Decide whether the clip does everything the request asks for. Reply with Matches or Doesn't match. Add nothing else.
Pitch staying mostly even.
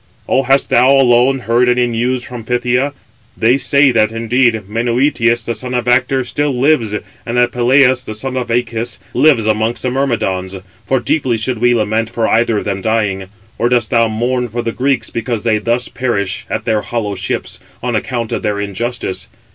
Matches